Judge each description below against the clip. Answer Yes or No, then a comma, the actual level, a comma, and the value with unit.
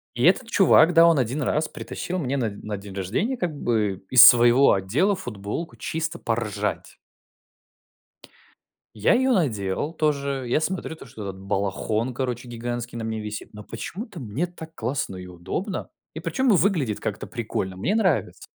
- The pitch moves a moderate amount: No, wide, 7.6 semitones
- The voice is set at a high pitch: No, low, 125 Hz